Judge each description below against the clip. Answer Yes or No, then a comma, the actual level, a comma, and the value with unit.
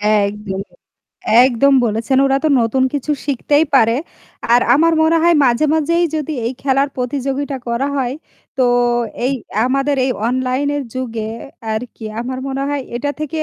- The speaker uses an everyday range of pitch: Yes, average, 3.3 semitones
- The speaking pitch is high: Yes, very high, 265 Hz